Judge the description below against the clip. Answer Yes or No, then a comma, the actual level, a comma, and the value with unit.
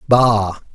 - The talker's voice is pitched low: Yes, low, 110 Hz